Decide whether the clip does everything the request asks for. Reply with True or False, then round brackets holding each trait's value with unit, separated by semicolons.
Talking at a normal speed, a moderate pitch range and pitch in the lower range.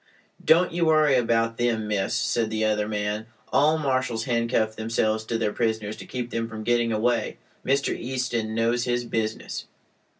False (165 wpm; 2.0 semitones; 115 Hz)